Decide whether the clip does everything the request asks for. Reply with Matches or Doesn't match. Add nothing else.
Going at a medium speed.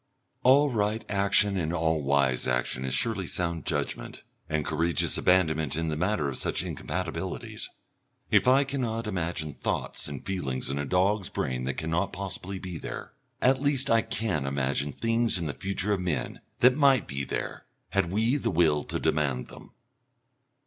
Matches